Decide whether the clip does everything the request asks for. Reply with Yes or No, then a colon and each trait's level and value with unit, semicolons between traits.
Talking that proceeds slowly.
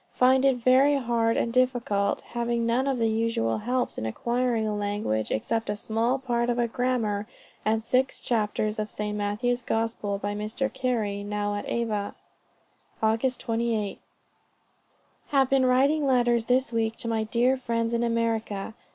No: average, 160 wpm